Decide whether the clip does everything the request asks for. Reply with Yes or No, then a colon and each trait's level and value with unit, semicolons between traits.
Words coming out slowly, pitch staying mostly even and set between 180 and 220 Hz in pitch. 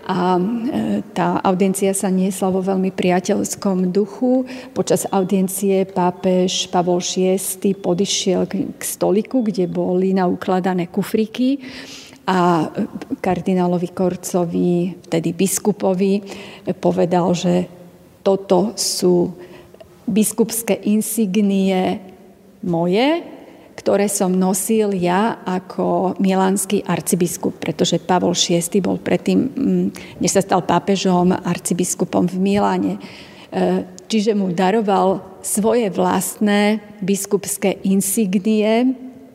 Yes: slow, 90 wpm; narrow, 2.3 semitones; high, 190 Hz